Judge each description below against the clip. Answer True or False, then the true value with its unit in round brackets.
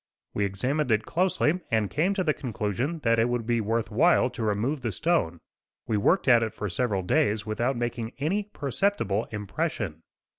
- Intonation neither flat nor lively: False (6.3 semitones)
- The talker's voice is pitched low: True (120 Hz)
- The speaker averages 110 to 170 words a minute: False (180 wpm)